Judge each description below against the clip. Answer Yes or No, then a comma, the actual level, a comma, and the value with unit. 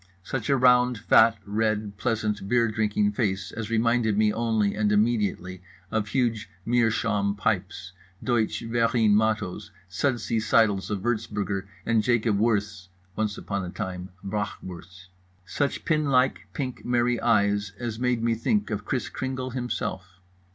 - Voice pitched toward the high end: No, low, 110 Hz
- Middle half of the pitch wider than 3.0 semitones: No, average, 2.7 semitones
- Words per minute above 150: No, average, 140 wpm